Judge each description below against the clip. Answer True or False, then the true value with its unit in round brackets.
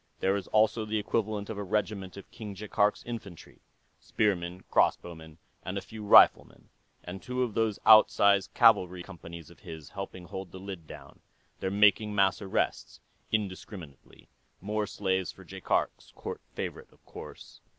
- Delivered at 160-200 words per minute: False (150 wpm)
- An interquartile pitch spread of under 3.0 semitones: True (2.6 semitones)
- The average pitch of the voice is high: False (100 Hz)